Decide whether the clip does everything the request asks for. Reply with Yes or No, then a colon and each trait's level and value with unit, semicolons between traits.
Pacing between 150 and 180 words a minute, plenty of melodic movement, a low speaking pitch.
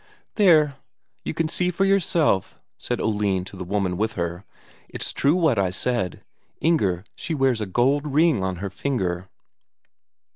Yes: average, 155 wpm; wide, 8.7 semitones; low, 115 Hz